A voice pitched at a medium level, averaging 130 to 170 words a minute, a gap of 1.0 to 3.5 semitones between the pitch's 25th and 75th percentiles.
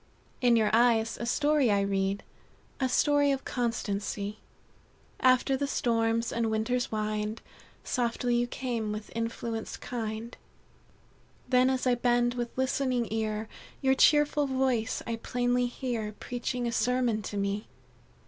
No: high, 240 Hz; slow, 135 wpm; narrow, 2.5 semitones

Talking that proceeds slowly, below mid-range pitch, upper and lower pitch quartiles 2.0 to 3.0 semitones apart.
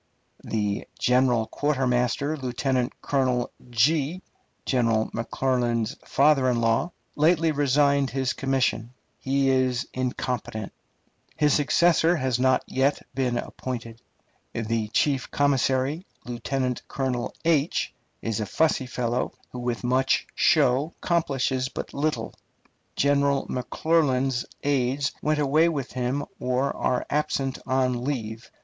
Yes: slow, 110 wpm; low, 130 Hz; narrow, 2.6 semitones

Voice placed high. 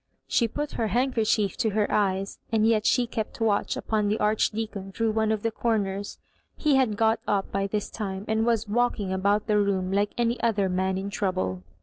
Yes: high, 210 Hz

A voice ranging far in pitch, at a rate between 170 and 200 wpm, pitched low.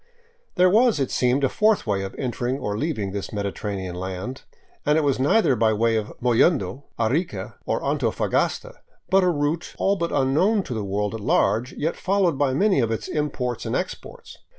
Yes: wide, 7.2 semitones; average, 185 wpm; low, 130 Hz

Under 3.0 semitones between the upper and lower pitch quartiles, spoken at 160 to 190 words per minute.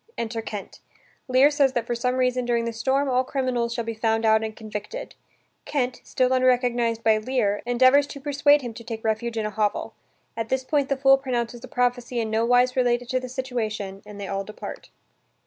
No: narrow, 2.5 semitones; fast, 205 wpm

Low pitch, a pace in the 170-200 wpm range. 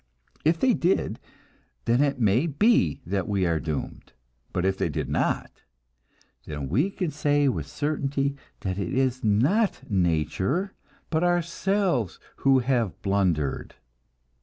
No: low, 130 Hz; slow, 135 wpm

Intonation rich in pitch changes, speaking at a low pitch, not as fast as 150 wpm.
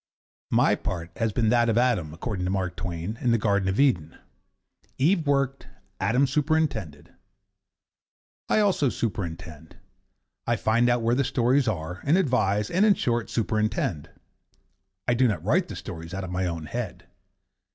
No: wide, 6.1 semitones; low, 110 Hz; average, 160 wpm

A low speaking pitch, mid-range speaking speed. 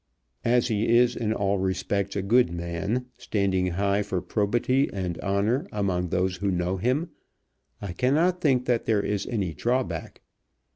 Yes: low, 100 Hz; average, 155 wpm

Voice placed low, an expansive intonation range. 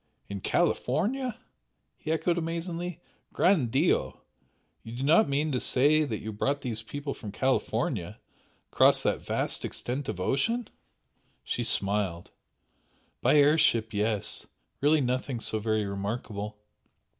Yes: low, 130 Hz; wide, 6.3 semitones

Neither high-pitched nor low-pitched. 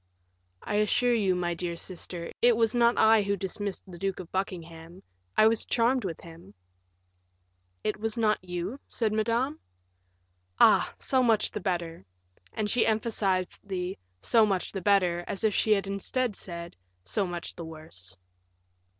No: high, 195 Hz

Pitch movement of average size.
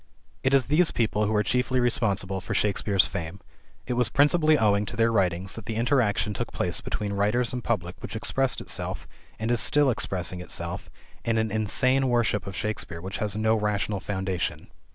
Yes: average, 3.8 semitones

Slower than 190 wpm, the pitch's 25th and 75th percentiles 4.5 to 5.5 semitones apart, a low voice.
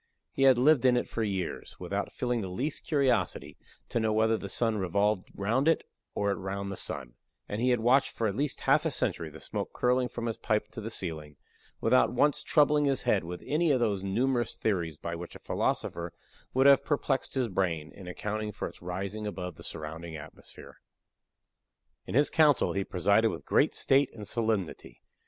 No: average, 195 wpm; average, 5.2 semitones; low, 110 Hz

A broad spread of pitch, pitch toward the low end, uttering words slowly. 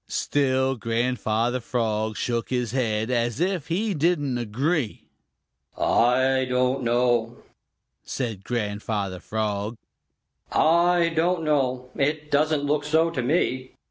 No: average, 4.5 semitones; low, 125 Hz; slow, 110 wpm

